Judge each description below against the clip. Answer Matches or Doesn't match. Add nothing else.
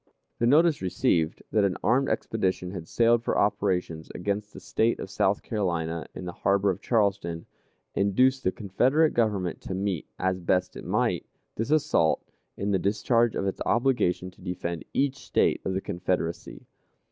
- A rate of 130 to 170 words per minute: Matches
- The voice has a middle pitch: Doesn't match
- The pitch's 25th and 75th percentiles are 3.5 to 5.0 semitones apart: Matches